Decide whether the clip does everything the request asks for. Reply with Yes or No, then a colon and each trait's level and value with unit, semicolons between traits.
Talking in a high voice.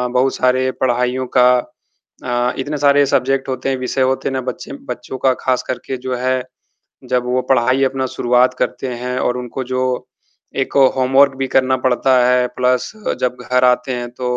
No: low, 130 Hz